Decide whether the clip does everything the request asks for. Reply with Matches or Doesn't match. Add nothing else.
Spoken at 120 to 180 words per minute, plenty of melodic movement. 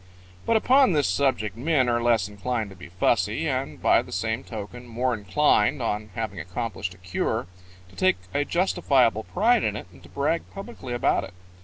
Doesn't match